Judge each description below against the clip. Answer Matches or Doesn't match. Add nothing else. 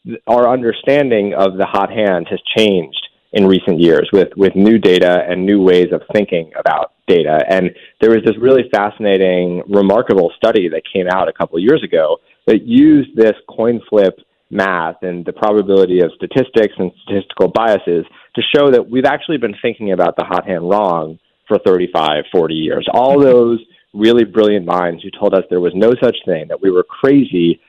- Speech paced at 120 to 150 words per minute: Doesn't match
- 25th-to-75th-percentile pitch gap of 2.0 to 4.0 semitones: Doesn't match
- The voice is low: Matches